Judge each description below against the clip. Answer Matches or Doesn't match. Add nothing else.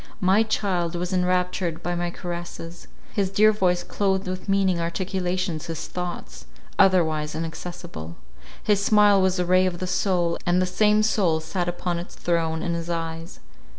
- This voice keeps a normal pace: Matches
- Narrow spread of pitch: Matches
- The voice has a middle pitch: Matches